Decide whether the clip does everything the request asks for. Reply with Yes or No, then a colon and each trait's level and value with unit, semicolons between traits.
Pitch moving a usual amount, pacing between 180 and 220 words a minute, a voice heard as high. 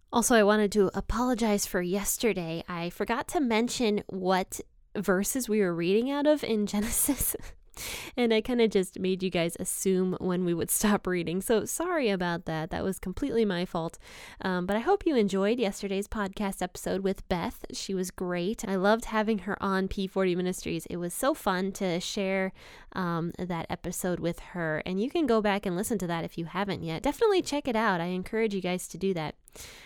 Yes: average, 3.4 semitones; average, 200 wpm; high, 195 Hz